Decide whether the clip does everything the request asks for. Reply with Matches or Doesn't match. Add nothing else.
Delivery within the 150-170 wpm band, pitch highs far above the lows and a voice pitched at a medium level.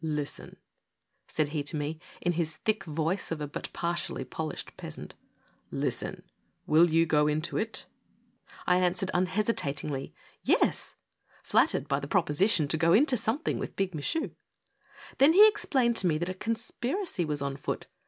Matches